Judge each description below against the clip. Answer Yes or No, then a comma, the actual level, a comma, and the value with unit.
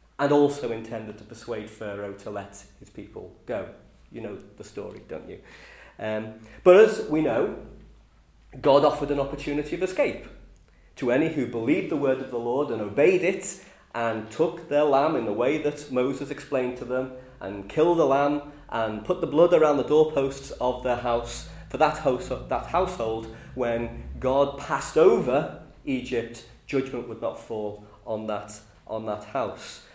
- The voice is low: Yes, low, 130 Hz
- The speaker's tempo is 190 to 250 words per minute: No, average, 165 wpm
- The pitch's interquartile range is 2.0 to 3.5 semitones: No, average, 4.5 semitones